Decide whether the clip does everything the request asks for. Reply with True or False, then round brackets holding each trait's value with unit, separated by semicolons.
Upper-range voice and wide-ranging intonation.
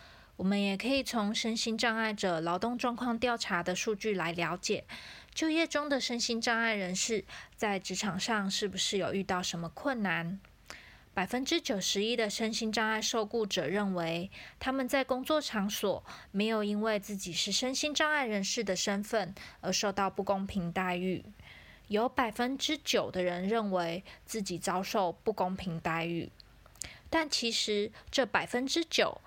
False (210 Hz; 4.0 semitones)